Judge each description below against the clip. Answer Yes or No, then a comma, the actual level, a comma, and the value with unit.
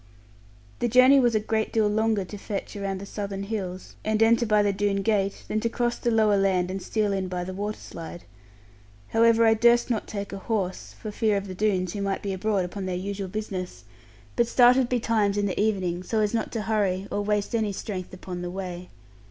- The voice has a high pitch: Yes, high, 205 Hz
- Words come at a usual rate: No, fast, 220 wpm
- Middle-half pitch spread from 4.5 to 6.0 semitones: No, narrow, 2.5 semitones